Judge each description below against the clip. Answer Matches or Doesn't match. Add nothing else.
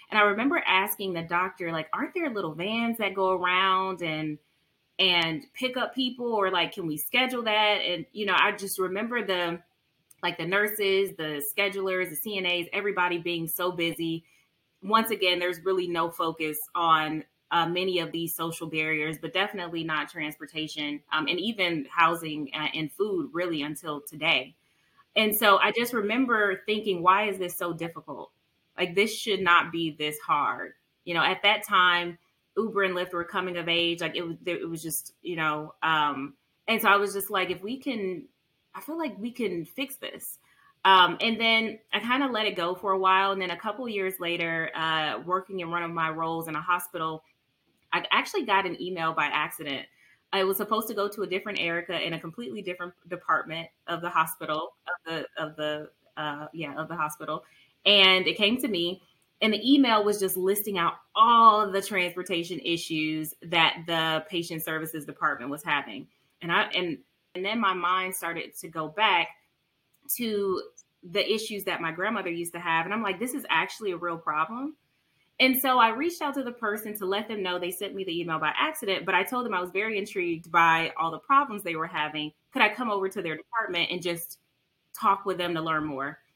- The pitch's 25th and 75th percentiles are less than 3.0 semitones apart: Doesn't match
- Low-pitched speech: Doesn't match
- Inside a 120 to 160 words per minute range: Doesn't match